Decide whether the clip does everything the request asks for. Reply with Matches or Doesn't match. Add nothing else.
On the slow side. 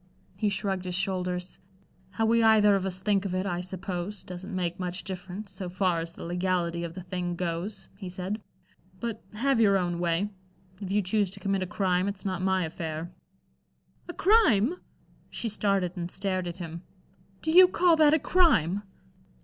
Doesn't match